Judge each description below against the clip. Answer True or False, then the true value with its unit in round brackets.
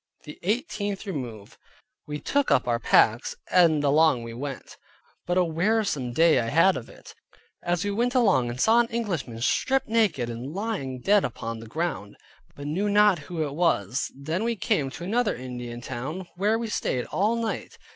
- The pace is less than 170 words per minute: False (180 wpm)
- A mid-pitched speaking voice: True (165 Hz)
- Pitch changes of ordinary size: False (8.5 semitones)